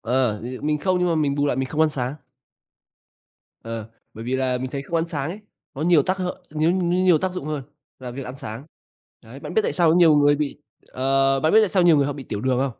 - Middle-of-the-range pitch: Yes, medium, 145 Hz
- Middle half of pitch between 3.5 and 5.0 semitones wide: Yes, average, 4.4 semitones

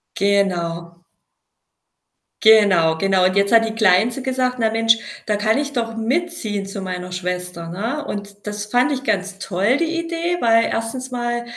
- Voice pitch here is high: Yes, high, 220 Hz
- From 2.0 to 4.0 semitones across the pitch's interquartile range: No, average, 4.4 semitones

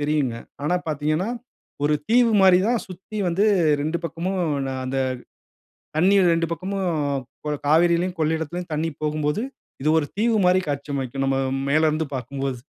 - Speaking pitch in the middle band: Yes, medium, 160 Hz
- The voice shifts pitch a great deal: No, average, 3.9 semitones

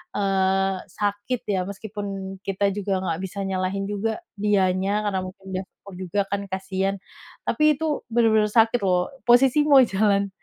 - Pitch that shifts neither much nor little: No, narrow, 2.1 semitones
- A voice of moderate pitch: No, high, 200 Hz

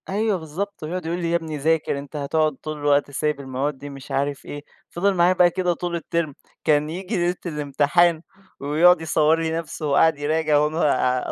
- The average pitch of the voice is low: No, medium, 155 Hz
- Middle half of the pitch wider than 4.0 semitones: No, average, 3.0 semitones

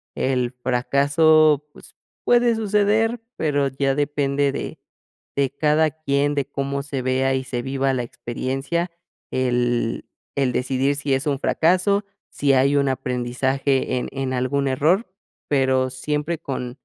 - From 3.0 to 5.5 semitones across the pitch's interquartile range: No, narrow, 2.4 semitones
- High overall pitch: No, medium, 140 Hz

